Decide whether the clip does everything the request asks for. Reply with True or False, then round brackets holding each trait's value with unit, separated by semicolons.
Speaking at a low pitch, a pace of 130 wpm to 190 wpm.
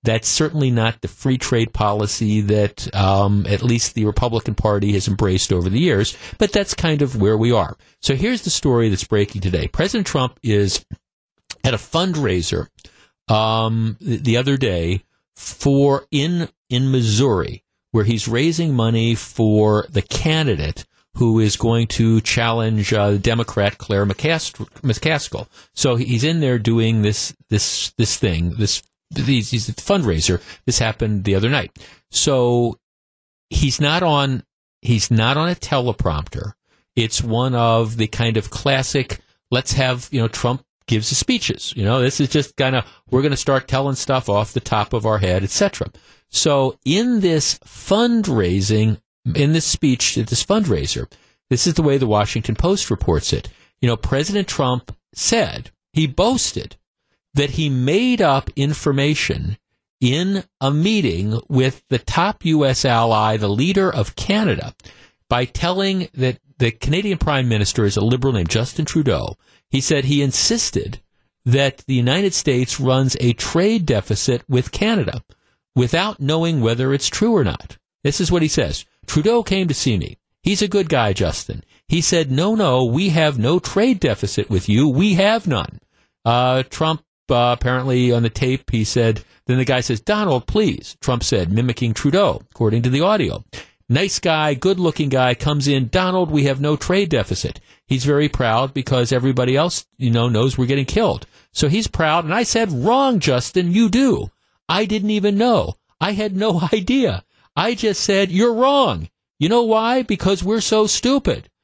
True (130 Hz; 165 wpm)